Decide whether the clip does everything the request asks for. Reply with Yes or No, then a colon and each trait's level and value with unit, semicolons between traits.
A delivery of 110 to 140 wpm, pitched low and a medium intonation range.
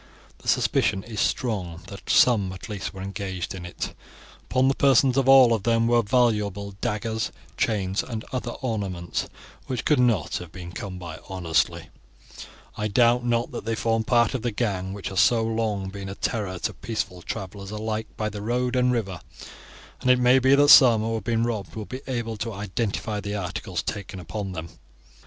No: average, 190 wpm; low, 110 Hz; average, 3.7 semitones